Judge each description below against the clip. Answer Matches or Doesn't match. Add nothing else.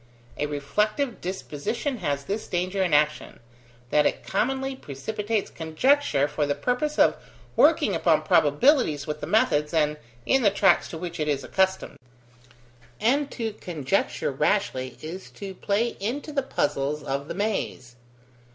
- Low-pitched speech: Doesn't match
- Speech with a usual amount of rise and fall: Doesn't match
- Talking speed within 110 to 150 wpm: Matches